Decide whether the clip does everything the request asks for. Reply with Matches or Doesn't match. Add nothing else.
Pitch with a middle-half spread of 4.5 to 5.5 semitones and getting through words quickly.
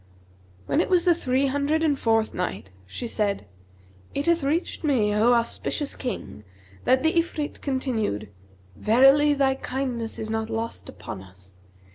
Doesn't match